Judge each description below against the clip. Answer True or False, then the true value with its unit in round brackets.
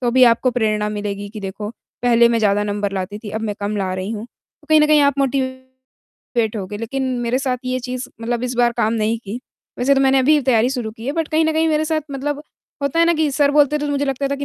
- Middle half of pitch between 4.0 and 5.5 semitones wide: True (4.5 semitones)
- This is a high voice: True (250 Hz)